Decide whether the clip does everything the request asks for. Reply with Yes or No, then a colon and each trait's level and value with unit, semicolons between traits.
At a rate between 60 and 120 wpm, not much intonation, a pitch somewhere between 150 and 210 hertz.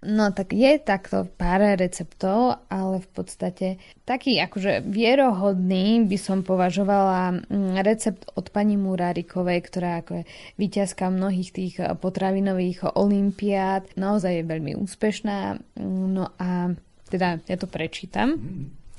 Yes: average, 115 wpm; narrow, 1.9 semitones; high, 190 Hz